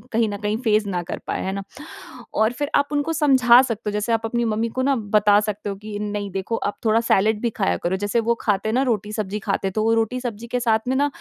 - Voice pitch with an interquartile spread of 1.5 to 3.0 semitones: Yes, narrow, 2.5 semitones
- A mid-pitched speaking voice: No, high, 220 Hz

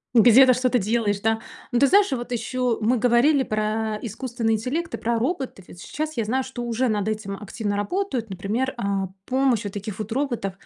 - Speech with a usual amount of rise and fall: Yes, average, 3.4 semitones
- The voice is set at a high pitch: Yes, high, 235 Hz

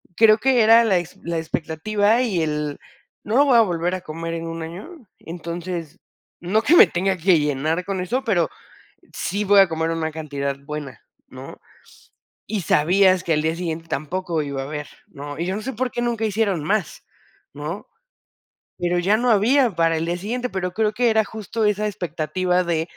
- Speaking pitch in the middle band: Yes, medium, 180 Hz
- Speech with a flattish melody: No, average, 4.9 semitones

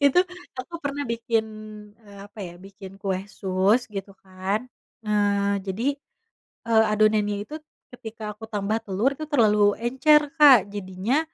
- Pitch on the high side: Yes, high, 210 Hz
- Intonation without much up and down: No, average, 3.1 semitones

